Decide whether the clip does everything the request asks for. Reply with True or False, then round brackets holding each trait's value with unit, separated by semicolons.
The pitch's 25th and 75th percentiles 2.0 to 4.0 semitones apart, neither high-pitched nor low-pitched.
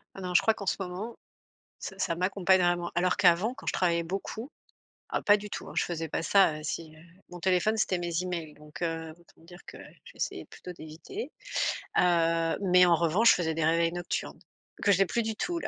True (2.8 semitones; 175 Hz)